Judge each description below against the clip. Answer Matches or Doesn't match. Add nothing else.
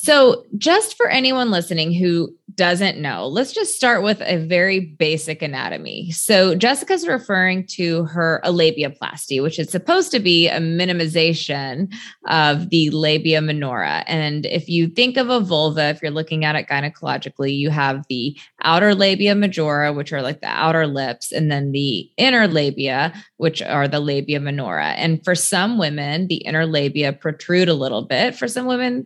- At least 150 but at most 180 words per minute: Matches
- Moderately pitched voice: Matches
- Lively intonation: Doesn't match